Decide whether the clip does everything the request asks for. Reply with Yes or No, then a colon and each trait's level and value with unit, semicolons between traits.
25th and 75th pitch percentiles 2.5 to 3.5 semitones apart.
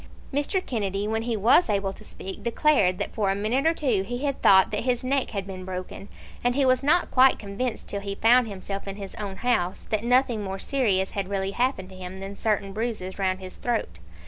No: average, 4.3 semitones